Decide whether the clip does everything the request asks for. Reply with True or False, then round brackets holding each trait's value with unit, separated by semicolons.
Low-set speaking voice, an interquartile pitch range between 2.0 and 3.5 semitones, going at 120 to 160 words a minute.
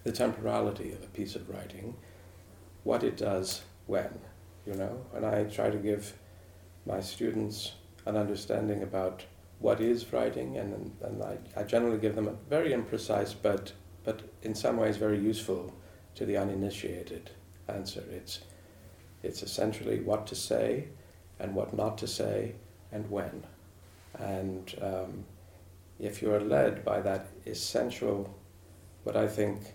True (95 Hz; 2.7 semitones; 145 wpm)